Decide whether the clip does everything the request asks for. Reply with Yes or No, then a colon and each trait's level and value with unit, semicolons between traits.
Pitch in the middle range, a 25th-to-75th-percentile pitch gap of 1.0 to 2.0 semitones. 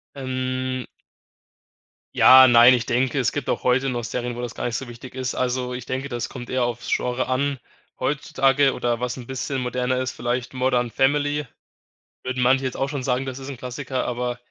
No: low, 130 Hz; narrow, 1.3 semitones